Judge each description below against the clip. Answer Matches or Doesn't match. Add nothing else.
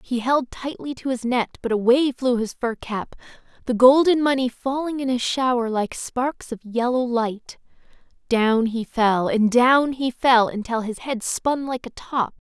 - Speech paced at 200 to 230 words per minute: Doesn't match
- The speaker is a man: Doesn't match